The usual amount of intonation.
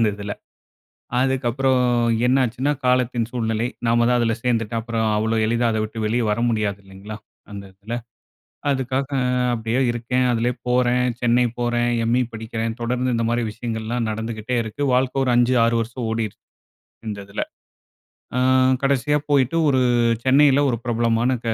No: narrow, 2.1 semitones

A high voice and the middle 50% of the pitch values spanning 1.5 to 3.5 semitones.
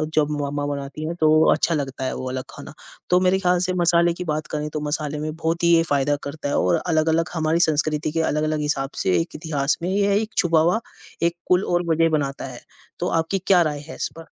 No: medium, 155 Hz; average, 2.7 semitones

